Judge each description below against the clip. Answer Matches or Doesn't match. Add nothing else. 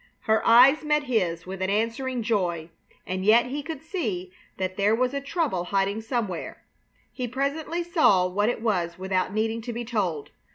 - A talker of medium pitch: Doesn't match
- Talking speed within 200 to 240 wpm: Doesn't match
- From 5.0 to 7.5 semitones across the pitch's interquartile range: Matches